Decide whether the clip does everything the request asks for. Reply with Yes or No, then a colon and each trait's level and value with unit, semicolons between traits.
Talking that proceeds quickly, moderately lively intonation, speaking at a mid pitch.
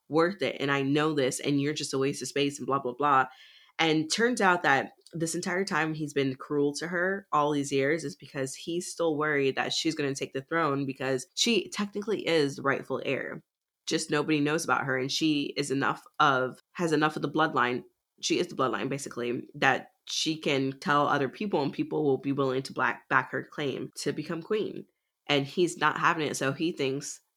Yes: fast, 215 wpm; average, 3.0 semitones; medium, 145 Hz